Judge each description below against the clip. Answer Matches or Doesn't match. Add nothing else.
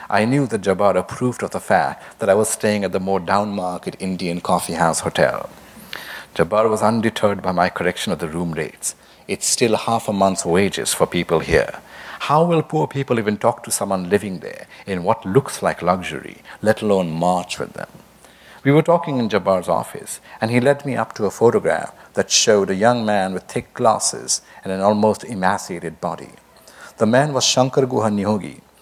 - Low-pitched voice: Matches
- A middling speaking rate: Matches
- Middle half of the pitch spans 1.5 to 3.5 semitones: Doesn't match